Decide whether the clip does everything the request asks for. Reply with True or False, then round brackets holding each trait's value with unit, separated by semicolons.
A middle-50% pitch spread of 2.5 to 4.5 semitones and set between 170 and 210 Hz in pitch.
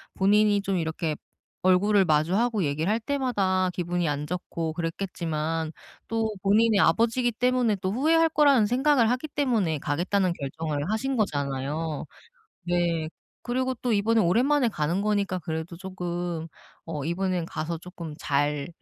False (5.6 semitones; 185 Hz)